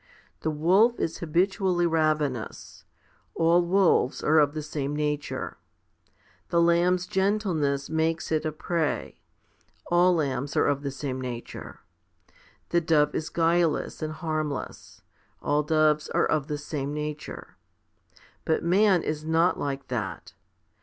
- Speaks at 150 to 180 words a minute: No, slow, 135 wpm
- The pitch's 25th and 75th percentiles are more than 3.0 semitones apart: No, narrow, 2.6 semitones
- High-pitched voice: No, medium, 155 Hz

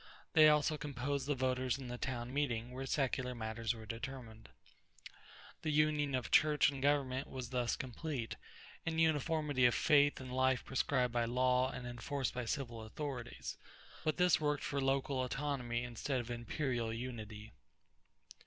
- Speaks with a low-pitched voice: Yes, low, 130 Hz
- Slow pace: No, average, 155 wpm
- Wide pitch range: No, average, 3.0 semitones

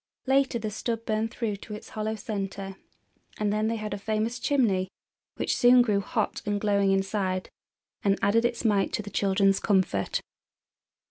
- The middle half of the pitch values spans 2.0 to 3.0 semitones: Yes, narrow, 2.4 semitones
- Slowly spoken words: No, average, 170 wpm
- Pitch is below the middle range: No, high, 210 Hz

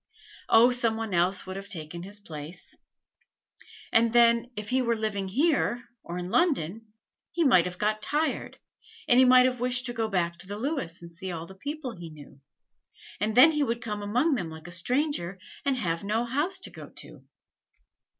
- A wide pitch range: Yes, wide, 5.7 semitones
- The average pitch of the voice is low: No, high, 220 Hz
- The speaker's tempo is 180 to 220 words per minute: Yes, average, 195 wpm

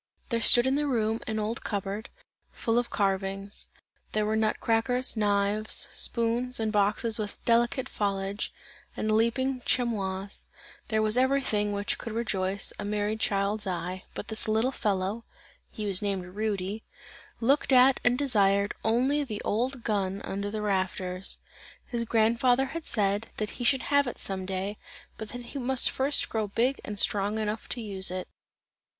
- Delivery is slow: No, average, 165 wpm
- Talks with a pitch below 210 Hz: No, high, 215 Hz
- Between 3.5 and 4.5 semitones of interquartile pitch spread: No, average, 3.1 semitones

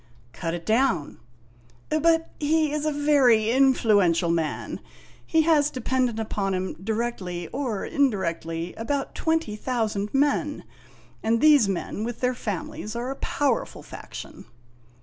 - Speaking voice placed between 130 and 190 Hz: No, high, 230 Hz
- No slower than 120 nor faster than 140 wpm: Yes, slow, 135 wpm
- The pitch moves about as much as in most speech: No, wide, 6.9 semitones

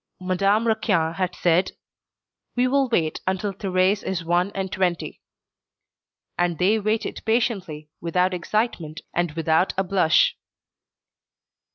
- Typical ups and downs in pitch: Yes, average, 3.3 semitones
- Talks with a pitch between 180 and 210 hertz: Yes, medium, 185 Hz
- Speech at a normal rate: No, slow, 120 wpm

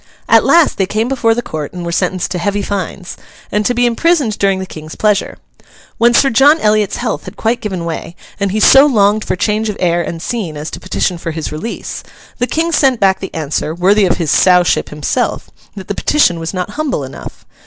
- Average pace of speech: No, fast, 215 wpm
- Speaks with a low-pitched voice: No, high, 200 Hz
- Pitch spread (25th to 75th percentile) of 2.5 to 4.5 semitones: No, average, 5.2 semitones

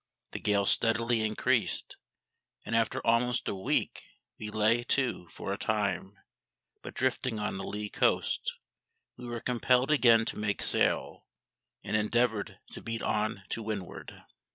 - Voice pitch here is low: Yes, low, 110 Hz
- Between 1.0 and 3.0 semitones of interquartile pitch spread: Yes, narrow, 2.4 semitones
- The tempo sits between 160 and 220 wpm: No, average, 145 wpm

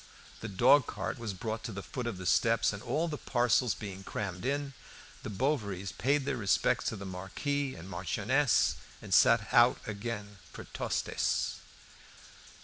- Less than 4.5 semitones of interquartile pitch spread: No, average, 4.9 semitones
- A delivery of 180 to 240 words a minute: No, average, 160 wpm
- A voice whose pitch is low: Yes, low, 110 Hz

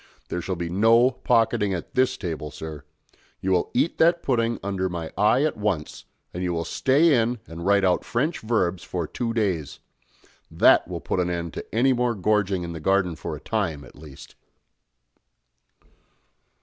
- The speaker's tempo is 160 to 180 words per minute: Yes, average, 175 wpm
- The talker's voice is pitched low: Yes, very low, 95 Hz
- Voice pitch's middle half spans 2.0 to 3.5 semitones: No, wide, 5.5 semitones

